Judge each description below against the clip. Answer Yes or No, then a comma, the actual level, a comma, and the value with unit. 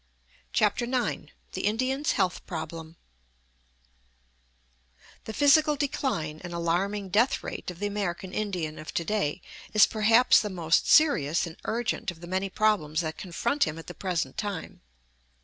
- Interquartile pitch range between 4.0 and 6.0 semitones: Yes, average, 4.7 semitones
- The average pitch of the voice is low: No, high, 190 Hz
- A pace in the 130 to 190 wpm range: Yes, average, 150 wpm